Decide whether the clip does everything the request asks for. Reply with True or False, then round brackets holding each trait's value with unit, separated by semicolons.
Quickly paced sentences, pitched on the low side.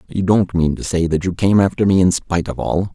True (285 wpm; 90 Hz)